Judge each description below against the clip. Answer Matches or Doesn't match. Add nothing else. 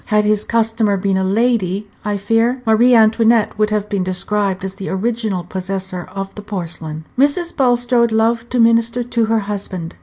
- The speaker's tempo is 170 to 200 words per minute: Matches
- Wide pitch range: Doesn't match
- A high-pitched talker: Matches